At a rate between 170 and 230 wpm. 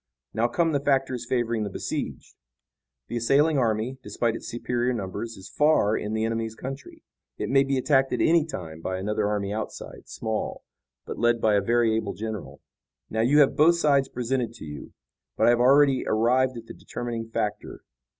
Yes: average, 185 wpm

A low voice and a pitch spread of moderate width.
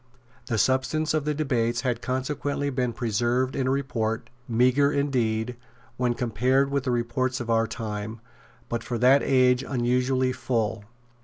No: low, 125 Hz; narrow, 2.2 semitones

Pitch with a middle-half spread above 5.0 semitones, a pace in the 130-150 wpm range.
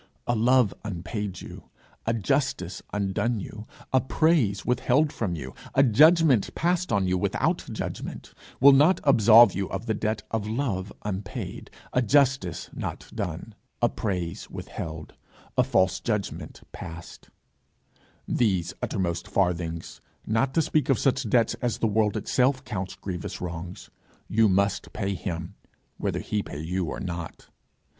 Yes: wide, 5.4 semitones; average, 145 wpm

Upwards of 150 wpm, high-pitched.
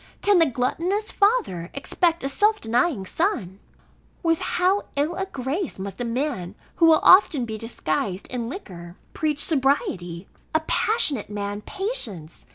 No: average, 145 wpm; very high, 275 Hz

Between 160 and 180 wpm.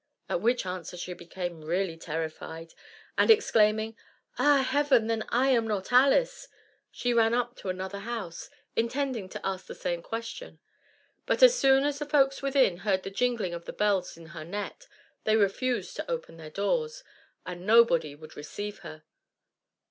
Yes: average, 165 wpm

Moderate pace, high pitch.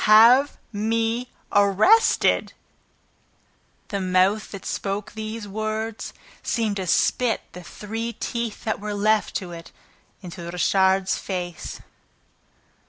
No: slow, 105 wpm; high, 210 Hz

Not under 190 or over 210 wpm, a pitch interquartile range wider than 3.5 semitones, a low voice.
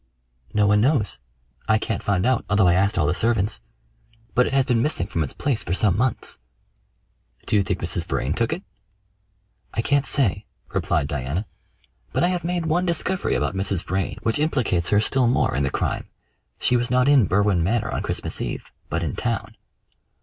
Yes: average, 195 wpm; wide, 5.5 semitones; low, 110 Hz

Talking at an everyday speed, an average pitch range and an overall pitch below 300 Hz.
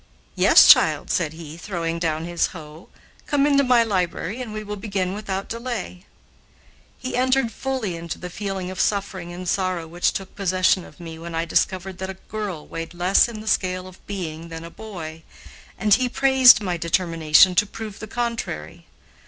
Yes: average, 180 wpm; average, 4.2 semitones; medium, 185 Hz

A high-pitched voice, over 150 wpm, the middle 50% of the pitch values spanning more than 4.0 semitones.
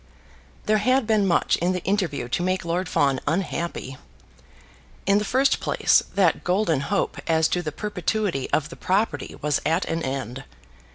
No: medium, 175 Hz; average, 165 wpm; average, 4.9 semitones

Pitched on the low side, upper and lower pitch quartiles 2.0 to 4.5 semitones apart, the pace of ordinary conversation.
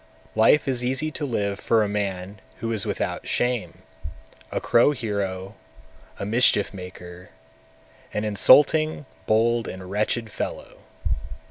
No: low, 110 Hz; average, 3.7 semitones; slow, 130 wpm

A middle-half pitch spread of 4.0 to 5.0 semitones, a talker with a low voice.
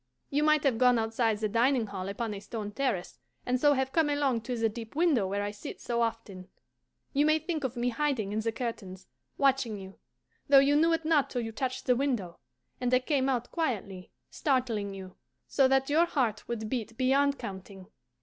No: average, 4.5 semitones; high, 245 Hz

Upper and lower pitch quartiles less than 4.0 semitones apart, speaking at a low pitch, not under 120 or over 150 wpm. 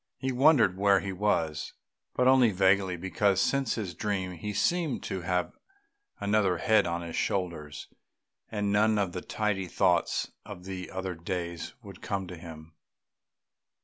Yes: average, 3.1 semitones; very low, 95 Hz; average, 145 wpm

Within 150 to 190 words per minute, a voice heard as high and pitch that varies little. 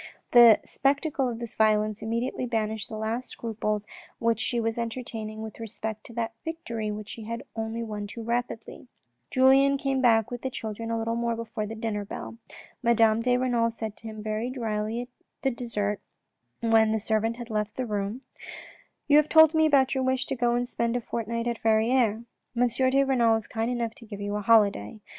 No: average, 200 wpm; high, 230 Hz; narrow, 2.0 semitones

